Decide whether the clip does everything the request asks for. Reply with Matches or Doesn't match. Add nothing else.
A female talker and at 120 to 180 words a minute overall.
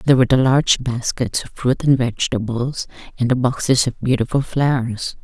Matches